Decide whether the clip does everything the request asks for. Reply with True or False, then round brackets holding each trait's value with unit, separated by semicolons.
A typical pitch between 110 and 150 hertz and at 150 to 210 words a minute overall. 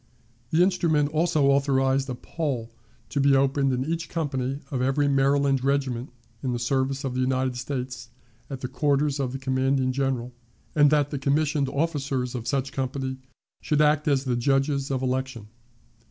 True (135 Hz; 170 wpm)